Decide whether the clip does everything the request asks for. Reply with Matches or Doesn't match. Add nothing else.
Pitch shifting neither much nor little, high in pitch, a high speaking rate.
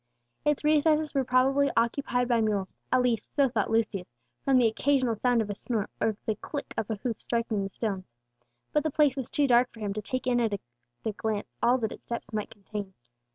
Matches